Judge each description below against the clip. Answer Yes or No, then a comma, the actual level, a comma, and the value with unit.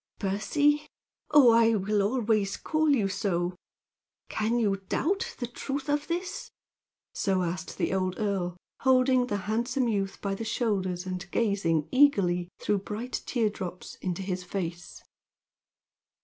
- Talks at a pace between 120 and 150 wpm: Yes, slow, 135 wpm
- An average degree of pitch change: Yes, average, 5.0 semitones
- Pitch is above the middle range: Yes, high, 210 Hz